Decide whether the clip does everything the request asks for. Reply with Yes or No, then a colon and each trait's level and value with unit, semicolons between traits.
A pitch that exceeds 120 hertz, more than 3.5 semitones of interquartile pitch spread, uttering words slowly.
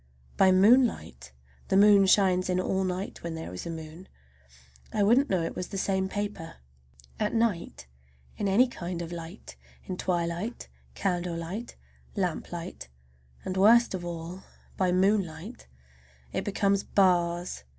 No: medium, 185 Hz; average, 3.0 semitones; slow, 130 wpm